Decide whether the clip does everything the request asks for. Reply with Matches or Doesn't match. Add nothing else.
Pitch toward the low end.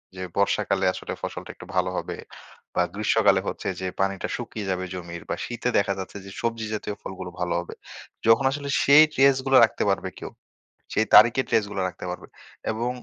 Matches